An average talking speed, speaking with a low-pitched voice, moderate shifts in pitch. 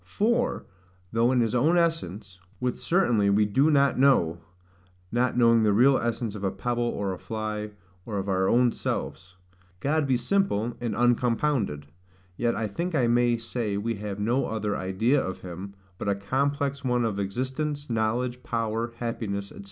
Yes: average, 170 wpm; low, 115 Hz; average, 4.1 semitones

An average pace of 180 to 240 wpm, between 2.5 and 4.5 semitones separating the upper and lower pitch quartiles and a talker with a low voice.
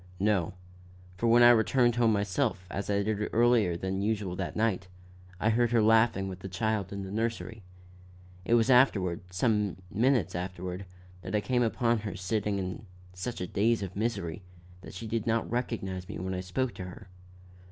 Yes: average, 185 wpm; average, 3.7 semitones; low, 105 Hz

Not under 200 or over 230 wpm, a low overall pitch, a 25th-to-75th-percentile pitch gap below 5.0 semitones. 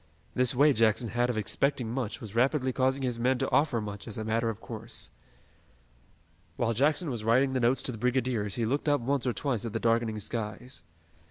Yes: fast, 205 wpm; low, 120 Hz; average, 2.8 semitones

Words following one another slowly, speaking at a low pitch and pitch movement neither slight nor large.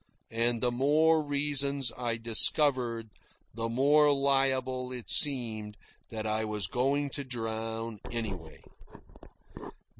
Yes: slow, 110 wpm; low, 125 Hz; average, 3.7 semitones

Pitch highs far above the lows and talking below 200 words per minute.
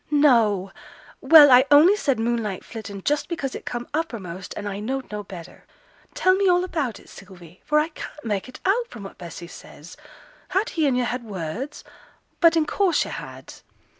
Yes: wide, 7.3 semitones; average, 190 wpm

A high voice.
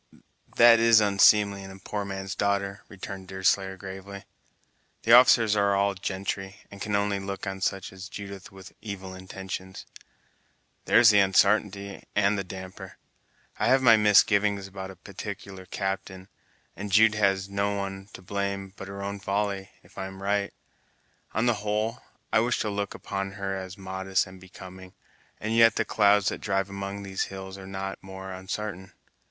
No: low, 100 Hz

